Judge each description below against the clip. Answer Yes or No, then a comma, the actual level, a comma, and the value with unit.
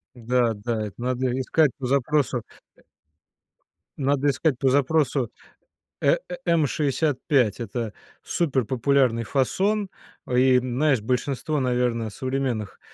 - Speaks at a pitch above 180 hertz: No, low, 130 Hz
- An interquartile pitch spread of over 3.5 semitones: No, average, 2.9 semitones